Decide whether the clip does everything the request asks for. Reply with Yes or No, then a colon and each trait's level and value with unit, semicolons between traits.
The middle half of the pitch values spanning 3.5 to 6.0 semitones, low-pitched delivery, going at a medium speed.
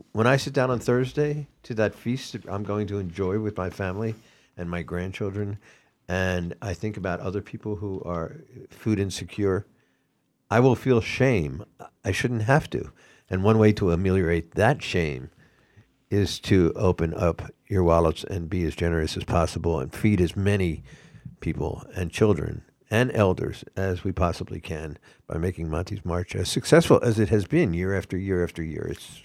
Yes: average, 4.2 semitones; low, 100 Hz; average, 175 wpm